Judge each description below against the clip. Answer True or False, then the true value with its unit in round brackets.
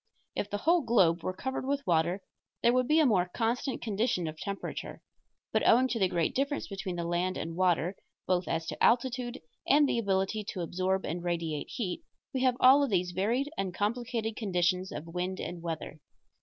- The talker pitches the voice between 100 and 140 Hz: False (195 Hz)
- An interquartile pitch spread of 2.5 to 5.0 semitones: False (5.5 semitones)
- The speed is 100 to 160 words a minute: False (195 wpm)